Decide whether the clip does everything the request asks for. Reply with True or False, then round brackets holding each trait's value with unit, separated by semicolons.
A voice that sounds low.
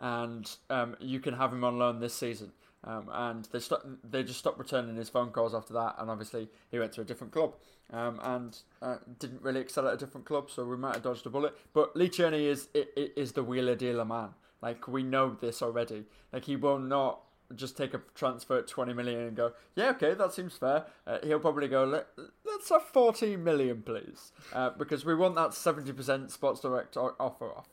True (130 Hz)